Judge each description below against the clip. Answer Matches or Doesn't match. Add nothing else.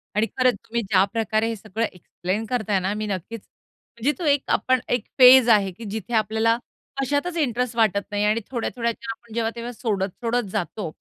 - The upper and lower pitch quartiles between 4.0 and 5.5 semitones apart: Doesn't match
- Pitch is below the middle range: Doesn't match